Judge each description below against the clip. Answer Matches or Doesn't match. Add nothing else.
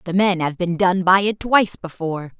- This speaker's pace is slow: Doesn't match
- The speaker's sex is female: Matches